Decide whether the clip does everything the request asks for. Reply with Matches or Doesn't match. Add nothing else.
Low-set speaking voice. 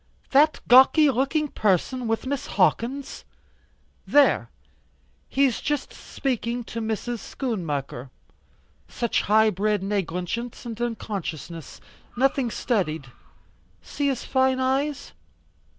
Doesn't match